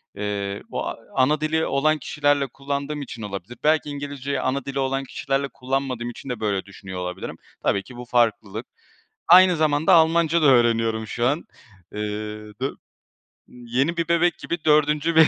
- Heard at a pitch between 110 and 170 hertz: Yes, low, 135 Hz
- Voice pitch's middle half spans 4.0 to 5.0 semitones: Yes, average, 4.5 semitones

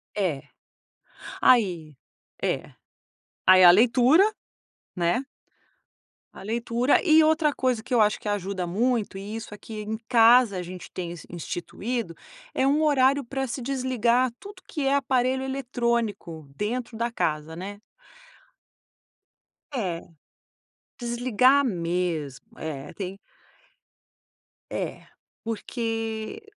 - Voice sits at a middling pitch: No, high, 230 Hz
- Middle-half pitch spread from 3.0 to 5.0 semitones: No, wide, 5.5 semitones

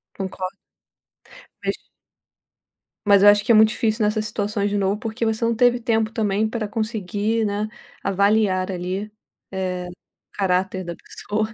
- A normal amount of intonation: No, narrow, 2.3 semitones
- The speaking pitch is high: Yes, high, 210 Hz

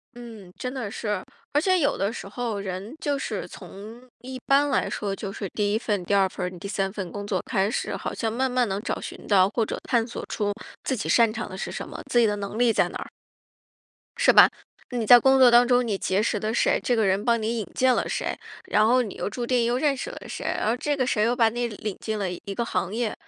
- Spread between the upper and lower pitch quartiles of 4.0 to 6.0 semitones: No, average, 3.4 semitones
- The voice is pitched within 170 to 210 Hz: No, high, 225 Hz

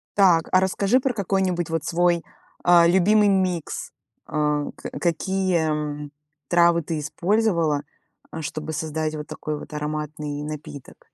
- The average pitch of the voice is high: No, medium, 165 Hz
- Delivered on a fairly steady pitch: No, average, 3.5 semitones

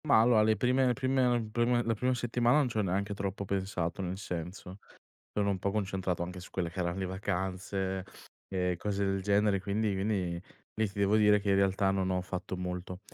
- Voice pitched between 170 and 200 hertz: No, low, 100 Hz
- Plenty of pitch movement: No, narrow, 2.5 semitones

